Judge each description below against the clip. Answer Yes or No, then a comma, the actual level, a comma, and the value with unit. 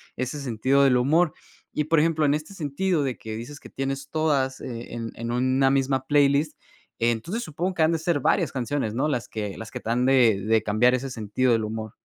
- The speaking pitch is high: No, low, 135 Hz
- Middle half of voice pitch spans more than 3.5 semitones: Yes, average, 4.2 semitones